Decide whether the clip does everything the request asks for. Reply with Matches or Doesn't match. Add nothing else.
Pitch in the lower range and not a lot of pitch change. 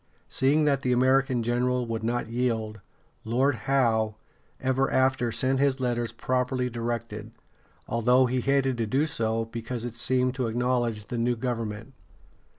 Matches